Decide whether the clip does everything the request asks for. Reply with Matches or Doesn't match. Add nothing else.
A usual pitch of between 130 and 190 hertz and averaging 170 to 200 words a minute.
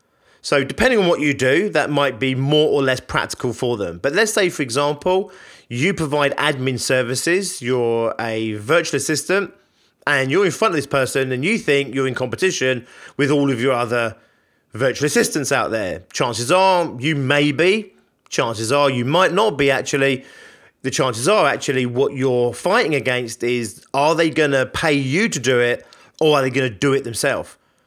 Matches